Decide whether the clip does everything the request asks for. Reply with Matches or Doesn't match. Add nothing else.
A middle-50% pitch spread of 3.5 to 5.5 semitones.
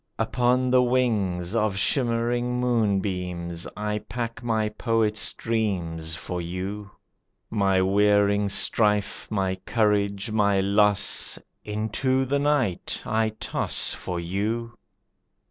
Doesn't match